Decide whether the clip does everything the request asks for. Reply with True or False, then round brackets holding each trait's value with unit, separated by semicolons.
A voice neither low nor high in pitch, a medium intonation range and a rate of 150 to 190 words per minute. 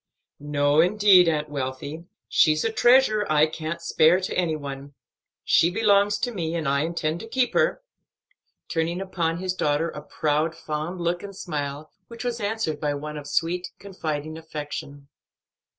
True (165 Hz; 4.1 semitones; 160 wpm)